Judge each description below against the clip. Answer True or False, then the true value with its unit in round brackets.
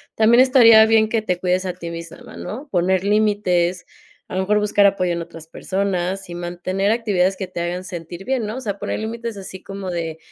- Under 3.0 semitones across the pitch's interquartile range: False (3.3 semitones)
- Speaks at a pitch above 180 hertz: True (190 Hz)